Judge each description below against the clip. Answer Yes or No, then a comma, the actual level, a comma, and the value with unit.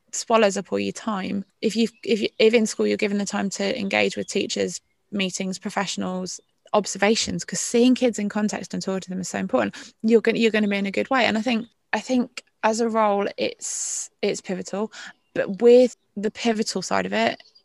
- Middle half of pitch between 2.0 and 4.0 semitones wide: Yes, average, 2.9 semitones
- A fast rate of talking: Yes, fast, 215 wpm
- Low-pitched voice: No, high, 210 Hz